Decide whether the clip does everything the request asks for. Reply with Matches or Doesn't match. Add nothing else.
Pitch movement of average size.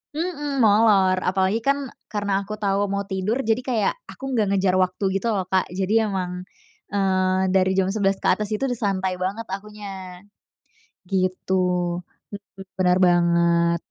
Doesn't match